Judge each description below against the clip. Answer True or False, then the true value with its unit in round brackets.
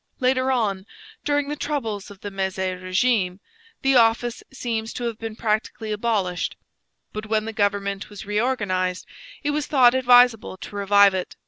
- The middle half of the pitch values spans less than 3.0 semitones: False (3.8 semitones)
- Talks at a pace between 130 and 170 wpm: True (155 wpm)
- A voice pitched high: True (215 Hz)